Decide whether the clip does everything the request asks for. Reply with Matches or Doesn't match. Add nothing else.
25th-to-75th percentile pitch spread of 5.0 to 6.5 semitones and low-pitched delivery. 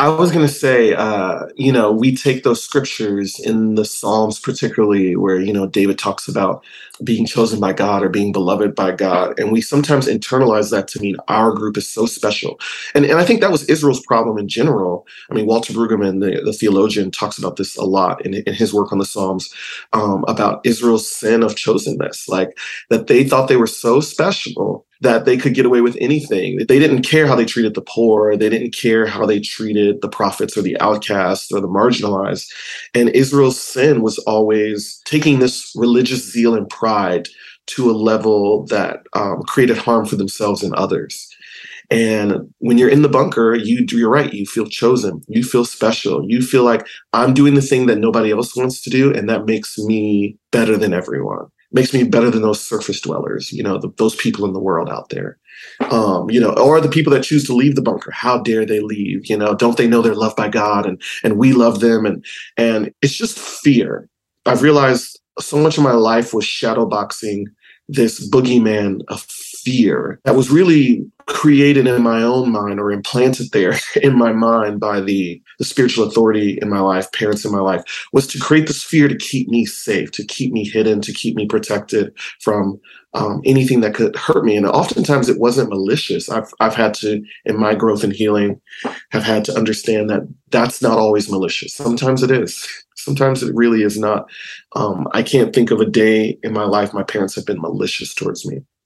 Doesn't match